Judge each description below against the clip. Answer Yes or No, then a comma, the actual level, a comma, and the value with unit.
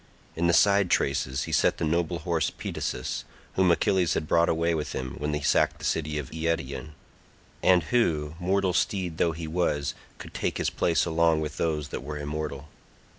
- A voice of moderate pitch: No, very low, 80 Hz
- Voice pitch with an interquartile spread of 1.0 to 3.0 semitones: Yes, narrow, 2.5 semitones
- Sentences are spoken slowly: No, average, 185 wpm